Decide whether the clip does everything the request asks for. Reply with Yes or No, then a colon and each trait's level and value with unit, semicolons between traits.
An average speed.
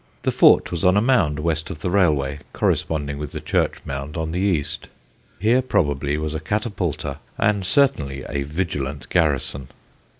Yes: average, 165 wpm